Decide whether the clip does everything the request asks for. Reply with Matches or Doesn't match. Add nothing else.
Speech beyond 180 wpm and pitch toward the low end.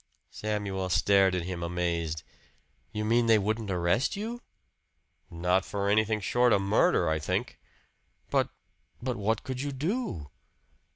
Doesn't match